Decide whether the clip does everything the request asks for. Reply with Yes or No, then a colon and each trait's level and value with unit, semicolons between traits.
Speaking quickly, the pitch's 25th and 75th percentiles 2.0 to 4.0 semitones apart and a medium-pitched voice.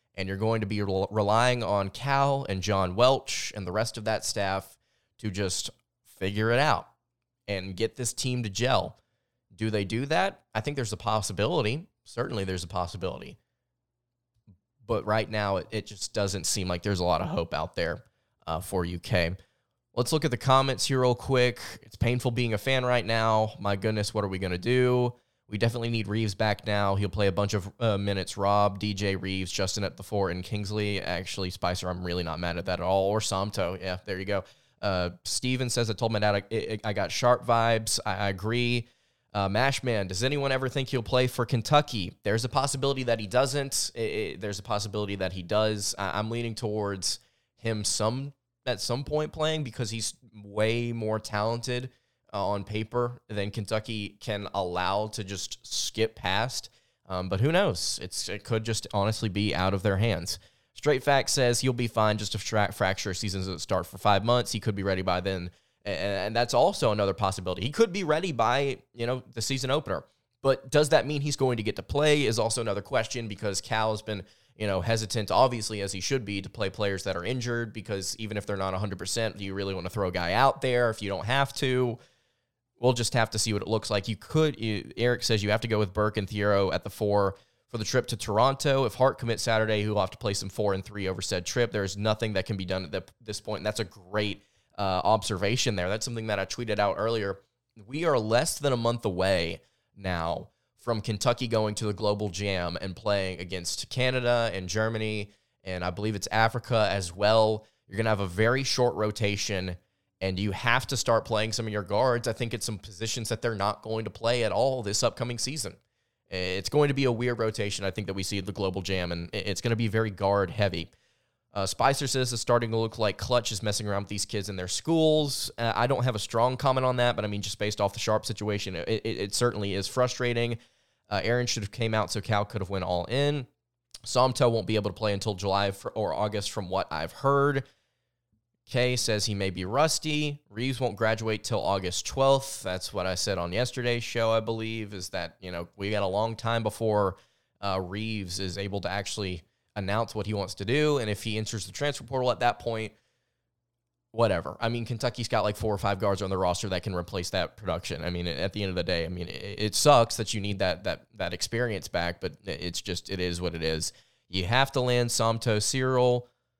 No: fast, 220 wpm; average, 3.4 semitones; low, 110 Hz